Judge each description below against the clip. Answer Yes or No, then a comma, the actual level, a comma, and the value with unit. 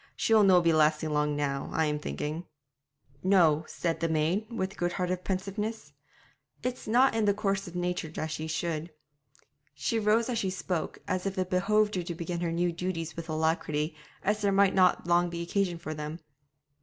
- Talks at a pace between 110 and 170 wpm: No, average, 185 wpm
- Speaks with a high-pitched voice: No, medium, 175 Hz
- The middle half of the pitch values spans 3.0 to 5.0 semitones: Yes, average, 3.6 semitones